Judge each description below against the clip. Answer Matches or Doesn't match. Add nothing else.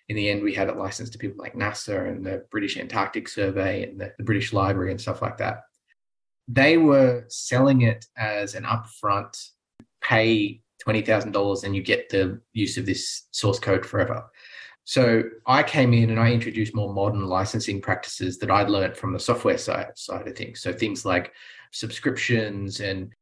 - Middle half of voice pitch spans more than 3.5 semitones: Doesn't match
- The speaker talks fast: Doesn't match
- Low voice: Matches